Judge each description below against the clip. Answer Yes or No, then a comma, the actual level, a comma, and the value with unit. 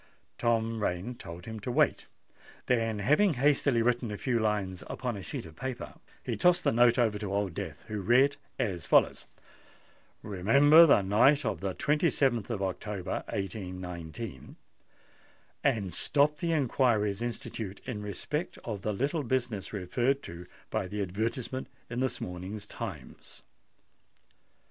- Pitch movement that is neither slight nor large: Yes, average, 4.8 semitones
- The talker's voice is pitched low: Yes, low, 110 Hz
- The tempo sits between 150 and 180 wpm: No, average, 140 wpm